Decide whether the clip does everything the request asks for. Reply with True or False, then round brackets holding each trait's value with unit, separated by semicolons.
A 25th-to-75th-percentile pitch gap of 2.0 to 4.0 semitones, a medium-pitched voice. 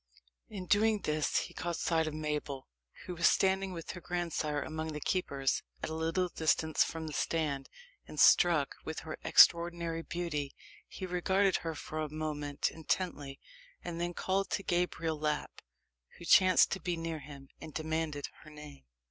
True (2.6 semitones; 160 Hz)